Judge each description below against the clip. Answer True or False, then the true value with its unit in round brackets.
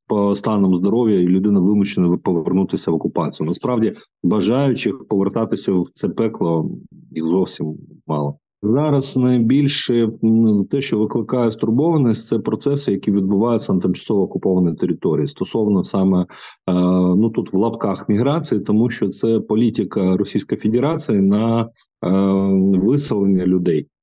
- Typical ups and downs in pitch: True (3.5 semitones)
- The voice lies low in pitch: True (100 Hz)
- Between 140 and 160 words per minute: False (120 wpm)